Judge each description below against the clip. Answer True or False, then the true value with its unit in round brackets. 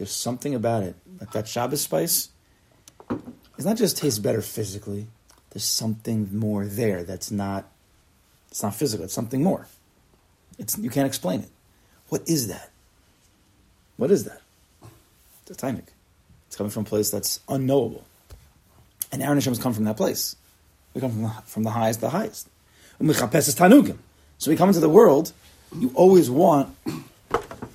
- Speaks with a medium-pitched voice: False (110 Hz)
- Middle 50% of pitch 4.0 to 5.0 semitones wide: True (4.3 semitones)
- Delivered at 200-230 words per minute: False (160 wpm)